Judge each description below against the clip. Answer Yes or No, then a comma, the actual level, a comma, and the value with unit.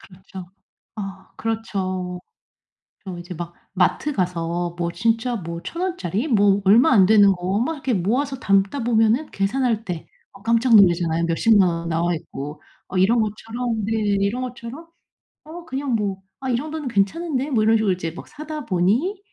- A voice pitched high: Yes, high, 210 Hz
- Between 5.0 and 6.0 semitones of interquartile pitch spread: Yes, wide, 5.5 semitones